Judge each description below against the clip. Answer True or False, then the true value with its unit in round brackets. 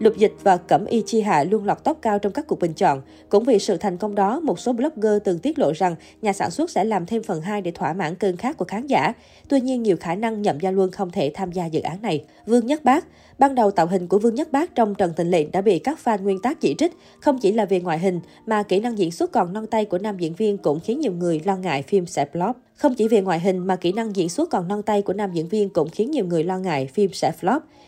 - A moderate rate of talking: False (295 wpm)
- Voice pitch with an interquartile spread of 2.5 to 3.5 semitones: False (4.1 semitones)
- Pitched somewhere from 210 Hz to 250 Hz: False (200 Hz)